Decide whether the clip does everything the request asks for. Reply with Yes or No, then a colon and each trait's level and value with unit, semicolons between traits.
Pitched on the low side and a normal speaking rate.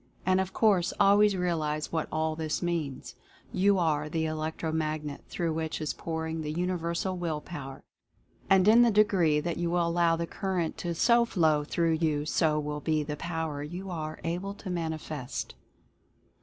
No: medium, 165 Hz; average, 170 wpm